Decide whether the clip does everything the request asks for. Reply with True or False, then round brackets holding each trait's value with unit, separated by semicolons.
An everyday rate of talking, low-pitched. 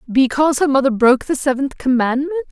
False (165 wpm; 275 Hz)